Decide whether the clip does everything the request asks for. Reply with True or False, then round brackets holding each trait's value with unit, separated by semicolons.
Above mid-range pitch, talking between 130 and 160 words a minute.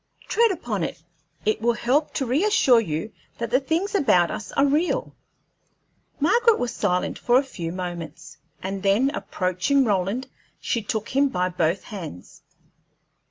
True (230 Hz; 150 wpm)